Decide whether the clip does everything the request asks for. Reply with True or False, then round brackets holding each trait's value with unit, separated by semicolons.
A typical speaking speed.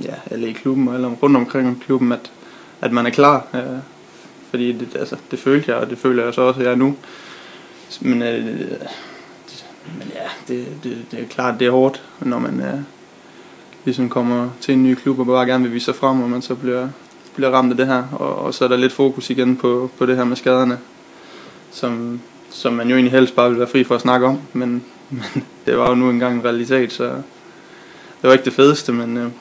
False (235 wpm)